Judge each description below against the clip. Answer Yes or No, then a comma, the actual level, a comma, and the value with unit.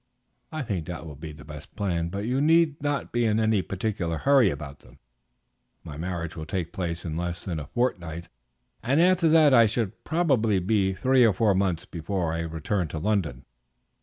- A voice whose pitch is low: Yes, very low, 95 Hz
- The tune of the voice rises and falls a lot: Yes, wide, 6.1 semitones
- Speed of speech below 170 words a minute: No, average, 195 wpm